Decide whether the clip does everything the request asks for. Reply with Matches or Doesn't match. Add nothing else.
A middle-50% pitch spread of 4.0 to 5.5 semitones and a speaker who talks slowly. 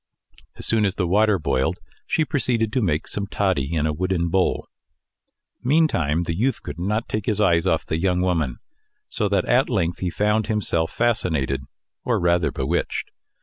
Doesn't match